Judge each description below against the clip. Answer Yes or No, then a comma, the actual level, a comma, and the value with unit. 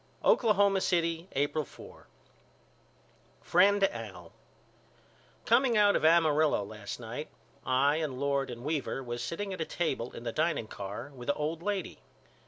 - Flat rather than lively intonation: No, wide, 5.6 semitones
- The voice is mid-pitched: Yes, medium, 155 Hz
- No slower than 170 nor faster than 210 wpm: No, average, 145 wpm